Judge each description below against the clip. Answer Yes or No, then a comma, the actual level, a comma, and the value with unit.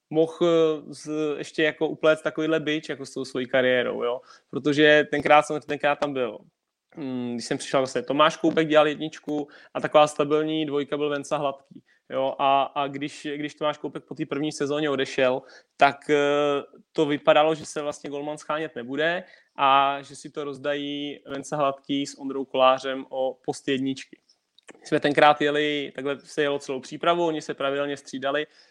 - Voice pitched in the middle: Yes, medium, 145 Hz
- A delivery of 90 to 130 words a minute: No, average, 165 wpm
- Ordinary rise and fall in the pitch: No, narrow, 1.7 semitones